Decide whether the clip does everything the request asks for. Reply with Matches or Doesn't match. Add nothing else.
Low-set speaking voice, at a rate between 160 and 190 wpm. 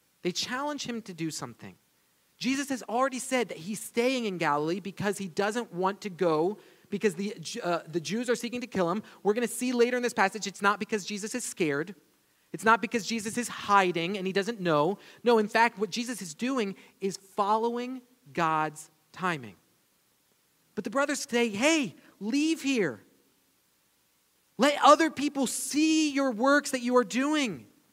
Doesn't match